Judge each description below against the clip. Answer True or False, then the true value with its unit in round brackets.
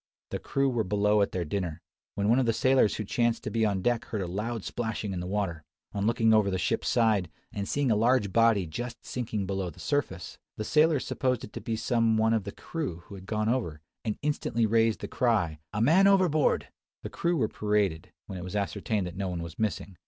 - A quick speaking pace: True (235 wpm)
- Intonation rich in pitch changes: False (3.7 semitones)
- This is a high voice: False (110 Hz)